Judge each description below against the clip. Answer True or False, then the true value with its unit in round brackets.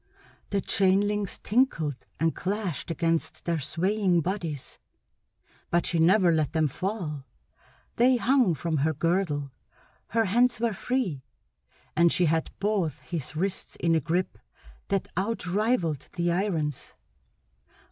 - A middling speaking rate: False (125 wpm)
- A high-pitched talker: False (175 Hz)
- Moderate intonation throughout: True (4.3 semitones)